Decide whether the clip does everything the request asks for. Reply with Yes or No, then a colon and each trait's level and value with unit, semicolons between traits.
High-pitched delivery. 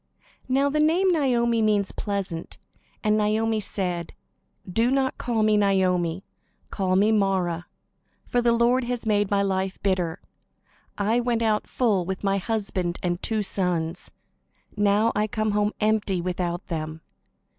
Yes: high, 205 Hz